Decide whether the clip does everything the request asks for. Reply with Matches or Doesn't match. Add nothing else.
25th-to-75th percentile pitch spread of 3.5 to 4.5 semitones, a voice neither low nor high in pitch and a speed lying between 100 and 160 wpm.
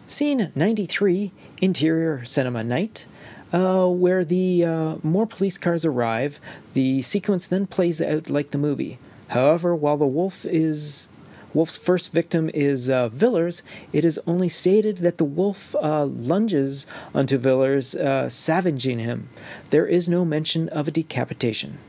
Matches